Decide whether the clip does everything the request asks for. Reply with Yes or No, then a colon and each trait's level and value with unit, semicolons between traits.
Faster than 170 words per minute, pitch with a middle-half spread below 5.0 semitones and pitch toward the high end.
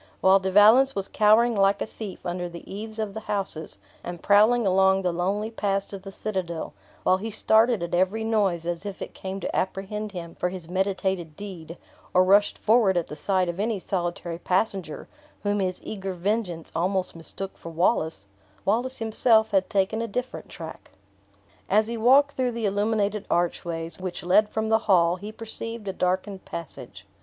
Yes: average, 180 wpm; average, 3.3 semitones; high, 195 Hz